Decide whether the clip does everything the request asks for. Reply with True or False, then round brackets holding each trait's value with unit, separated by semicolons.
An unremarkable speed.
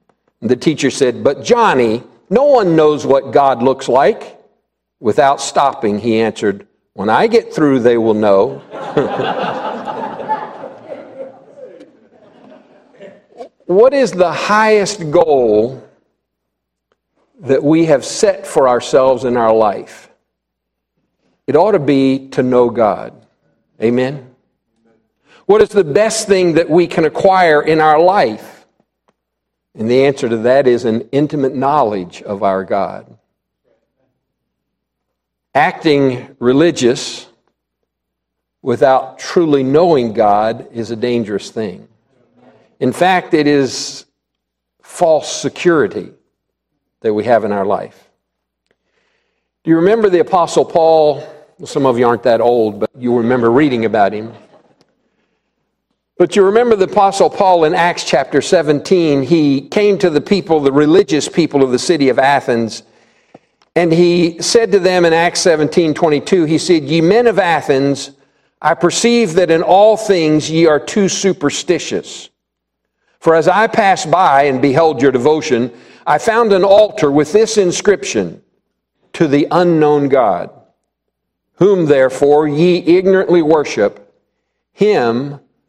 False (130 wpm)